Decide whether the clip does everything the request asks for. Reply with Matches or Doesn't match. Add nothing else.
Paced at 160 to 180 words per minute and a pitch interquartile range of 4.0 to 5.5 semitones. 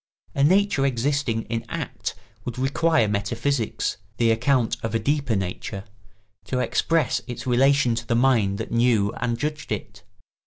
Doesn't match